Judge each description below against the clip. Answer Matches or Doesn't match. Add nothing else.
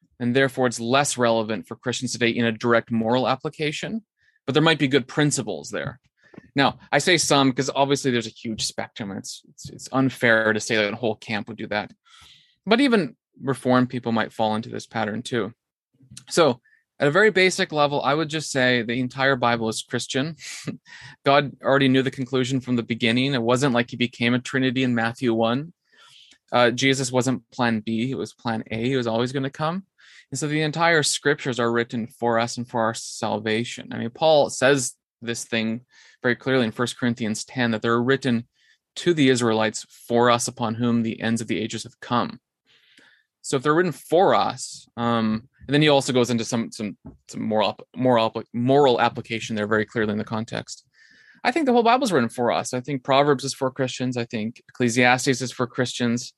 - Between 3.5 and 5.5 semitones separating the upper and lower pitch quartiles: Doesn't match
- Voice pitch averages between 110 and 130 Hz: Matches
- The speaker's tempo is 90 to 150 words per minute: Doesn't match